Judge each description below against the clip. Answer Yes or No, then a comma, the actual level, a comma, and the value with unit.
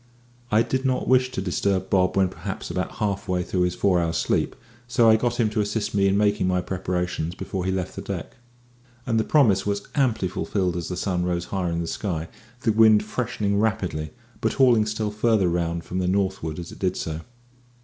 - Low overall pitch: Yes, very low, 95 Hz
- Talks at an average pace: No, fast, 210 wpm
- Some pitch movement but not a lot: Yes, average, 3.4 semitones